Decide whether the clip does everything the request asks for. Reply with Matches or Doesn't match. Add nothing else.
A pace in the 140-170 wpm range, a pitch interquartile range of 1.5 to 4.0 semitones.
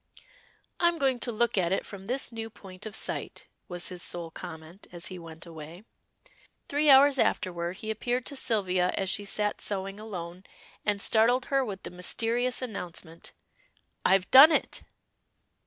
Doesn't match